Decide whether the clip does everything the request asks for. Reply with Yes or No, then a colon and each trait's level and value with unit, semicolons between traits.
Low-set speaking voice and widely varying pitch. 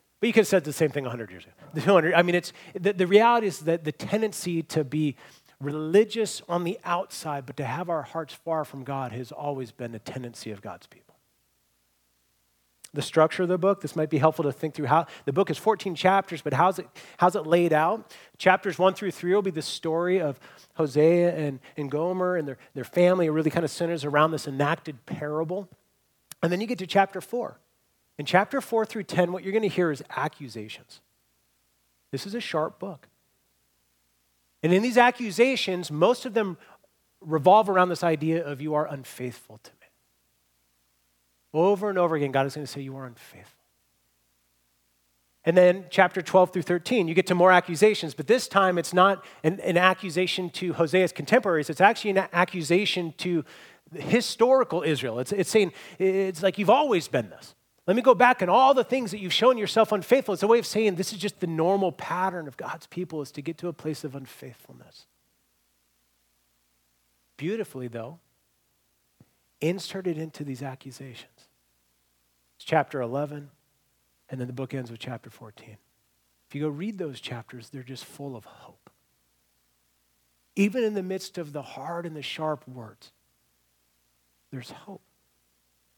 No: medium, 160 Hz; wide, 7.4 semitones